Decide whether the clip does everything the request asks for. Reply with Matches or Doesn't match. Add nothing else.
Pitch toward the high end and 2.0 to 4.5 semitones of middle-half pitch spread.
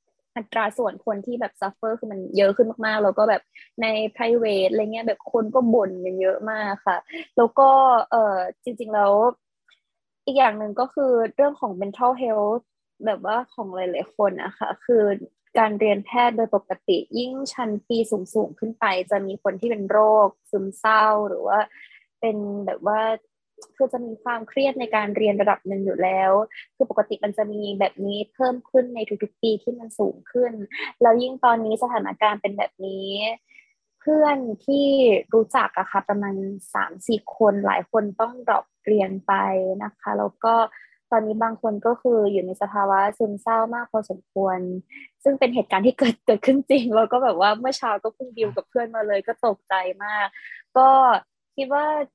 Matches